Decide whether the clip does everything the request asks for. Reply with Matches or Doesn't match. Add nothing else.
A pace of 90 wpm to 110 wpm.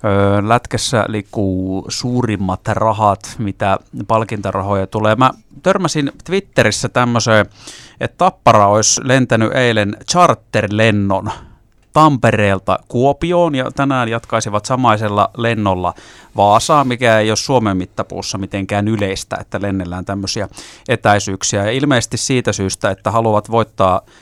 Matches